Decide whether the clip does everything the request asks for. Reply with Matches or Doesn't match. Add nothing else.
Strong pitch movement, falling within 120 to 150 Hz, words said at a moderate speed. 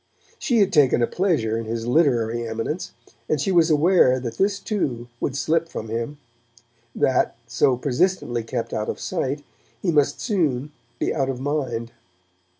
Matches